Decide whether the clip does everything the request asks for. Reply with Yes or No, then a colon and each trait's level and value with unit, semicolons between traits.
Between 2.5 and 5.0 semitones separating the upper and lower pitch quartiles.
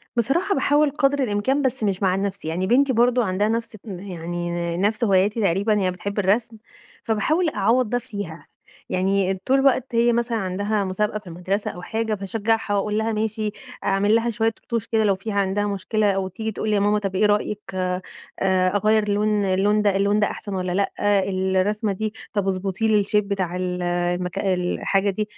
Yes: average, 2.8 semitones